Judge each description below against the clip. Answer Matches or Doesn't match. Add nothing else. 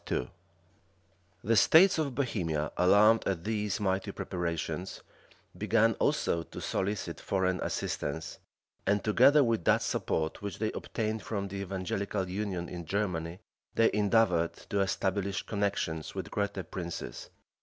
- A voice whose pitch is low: Matches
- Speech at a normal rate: Doesn't match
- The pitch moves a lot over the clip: Doesn't match